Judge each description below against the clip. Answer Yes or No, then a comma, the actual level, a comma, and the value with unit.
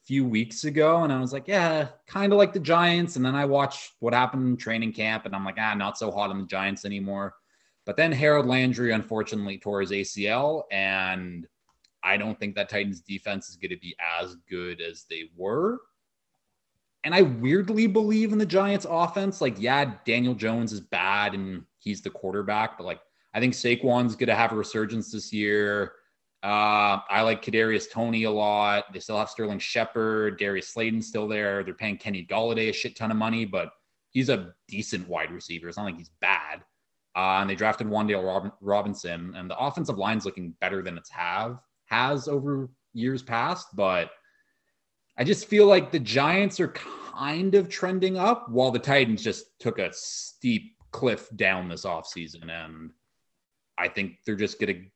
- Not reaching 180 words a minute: No, average, 190 wpm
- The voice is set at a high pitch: No, low, 110 Hz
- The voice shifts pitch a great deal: Yes, wide, 6.0 semitones